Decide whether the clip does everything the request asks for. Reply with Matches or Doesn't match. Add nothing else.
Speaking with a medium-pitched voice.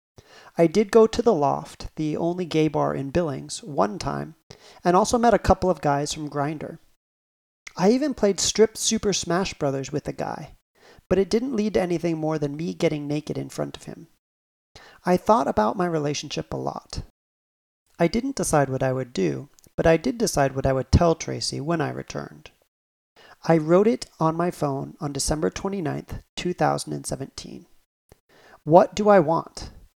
Matches